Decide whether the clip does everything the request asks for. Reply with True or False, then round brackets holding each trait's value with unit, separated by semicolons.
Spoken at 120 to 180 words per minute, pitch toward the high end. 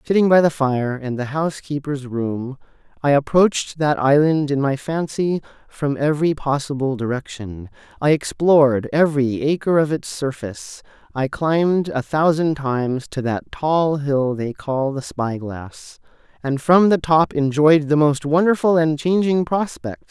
False (150 wpm; 145 Hz)